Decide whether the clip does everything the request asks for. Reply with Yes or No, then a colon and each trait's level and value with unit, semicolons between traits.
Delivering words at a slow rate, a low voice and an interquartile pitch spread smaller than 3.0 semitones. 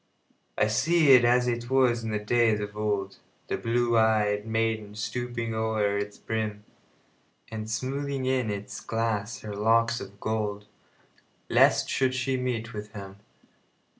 Yes: slow, 130 wpm; low, 110 Hz; narrow, 2.6 semitones